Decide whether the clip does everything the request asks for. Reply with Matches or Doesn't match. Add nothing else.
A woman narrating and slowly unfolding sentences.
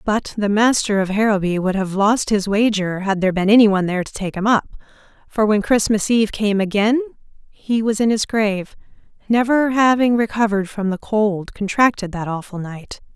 Doesn't match